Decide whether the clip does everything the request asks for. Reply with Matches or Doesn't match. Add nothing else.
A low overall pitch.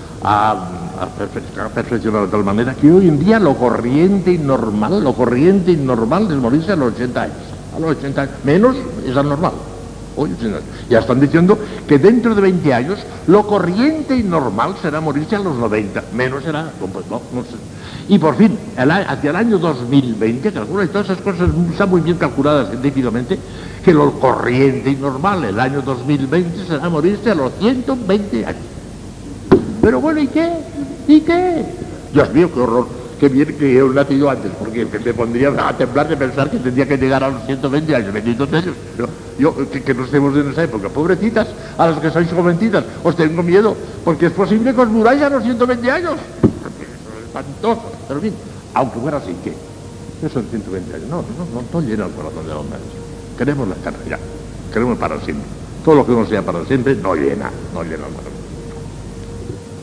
Doesn't match